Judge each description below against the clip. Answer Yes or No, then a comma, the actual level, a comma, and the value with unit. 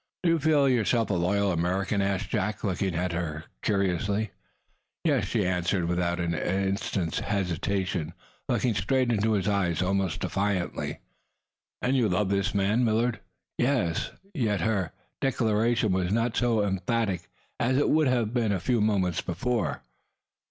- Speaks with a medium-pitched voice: No, low, 100 Hz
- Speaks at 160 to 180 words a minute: No, average, 145 wpm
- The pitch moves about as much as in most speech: Yes, average, 4.1 semitones